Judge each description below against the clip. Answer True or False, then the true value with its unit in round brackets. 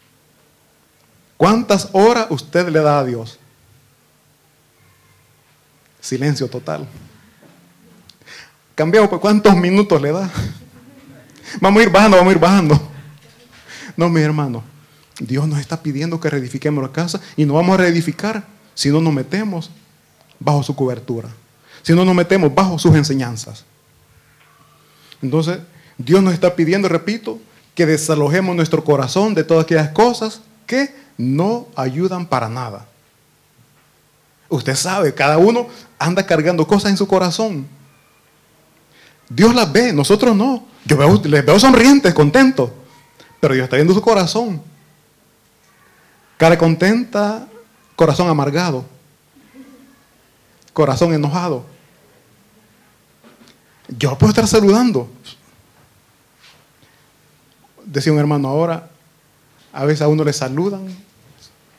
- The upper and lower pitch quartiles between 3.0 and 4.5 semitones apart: False (5.1 semitones)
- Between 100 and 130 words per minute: True (115 wpm)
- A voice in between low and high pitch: True (165 Hz)